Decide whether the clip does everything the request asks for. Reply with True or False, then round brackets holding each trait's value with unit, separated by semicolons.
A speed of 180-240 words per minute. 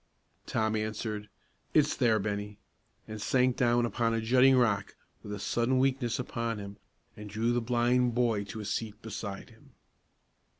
False (160 wpm)